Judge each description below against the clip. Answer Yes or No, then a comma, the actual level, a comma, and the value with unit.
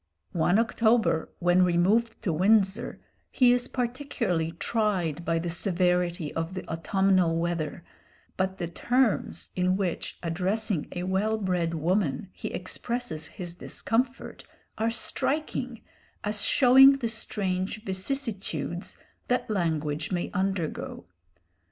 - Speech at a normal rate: No, slow, 115 wpm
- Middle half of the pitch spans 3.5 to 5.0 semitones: Yes, average, 4.7 semitones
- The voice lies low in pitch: No, high, 190 Hz